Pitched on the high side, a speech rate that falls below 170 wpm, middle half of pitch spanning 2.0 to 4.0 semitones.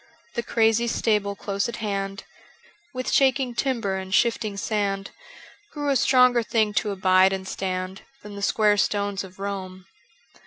Yes: high, 205 Hz; average, 150 wpm; average, 3.3 semitones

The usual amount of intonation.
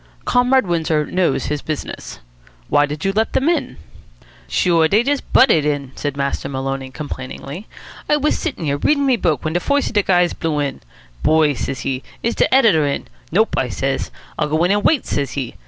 No: wide, 7.5 semitones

